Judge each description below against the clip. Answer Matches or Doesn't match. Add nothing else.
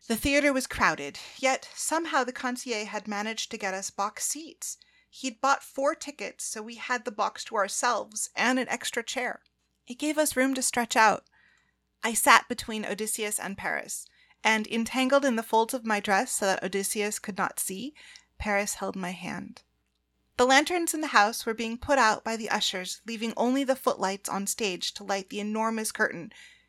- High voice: Matches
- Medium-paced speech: Matches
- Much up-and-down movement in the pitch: Doesn't match